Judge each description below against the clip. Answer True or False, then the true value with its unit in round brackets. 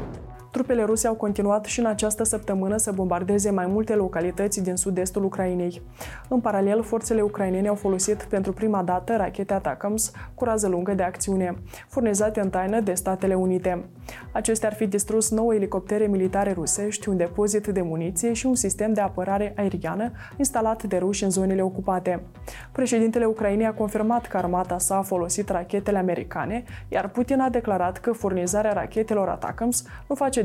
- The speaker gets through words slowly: False (165 wpm)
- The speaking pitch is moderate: False (205 Hz)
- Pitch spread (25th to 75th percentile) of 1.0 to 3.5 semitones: True (2.8 semitones)